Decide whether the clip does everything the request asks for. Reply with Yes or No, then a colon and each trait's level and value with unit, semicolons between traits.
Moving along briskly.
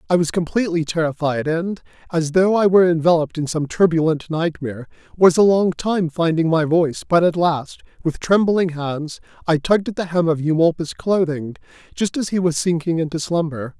No: average, 185 wpm